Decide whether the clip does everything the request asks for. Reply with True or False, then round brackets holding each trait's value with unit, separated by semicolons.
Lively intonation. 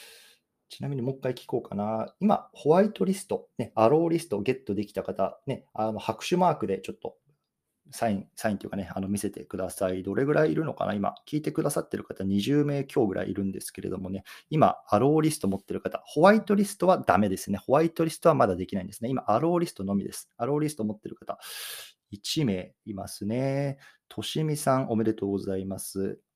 True (7.2 semitones)